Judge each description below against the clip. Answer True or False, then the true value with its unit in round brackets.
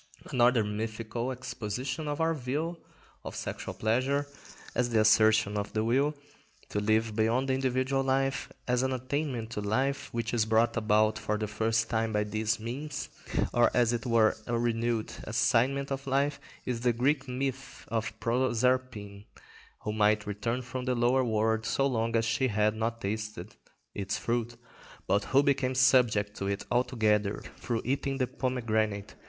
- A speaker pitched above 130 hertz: False (120 Hz)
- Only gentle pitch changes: False (3.1 semitones)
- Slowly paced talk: False (160 wpm)